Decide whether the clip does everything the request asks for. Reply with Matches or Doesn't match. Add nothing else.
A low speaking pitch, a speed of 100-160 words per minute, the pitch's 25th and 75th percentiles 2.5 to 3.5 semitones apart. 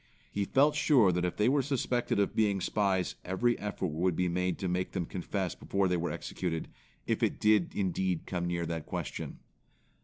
Doesn't match